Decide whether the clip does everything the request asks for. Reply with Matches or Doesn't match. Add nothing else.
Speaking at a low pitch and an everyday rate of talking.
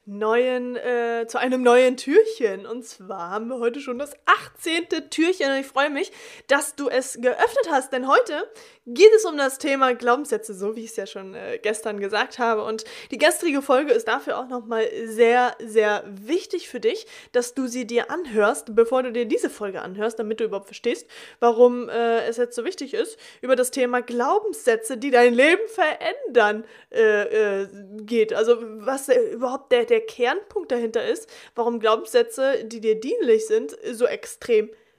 Doesn't match